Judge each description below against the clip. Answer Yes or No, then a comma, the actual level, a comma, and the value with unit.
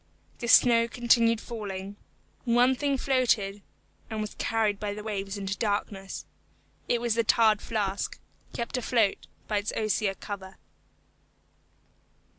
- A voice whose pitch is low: No, high, 215 Hz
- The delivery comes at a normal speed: No, slow, 130 wpm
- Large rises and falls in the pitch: No, narrow, 2.6 semitones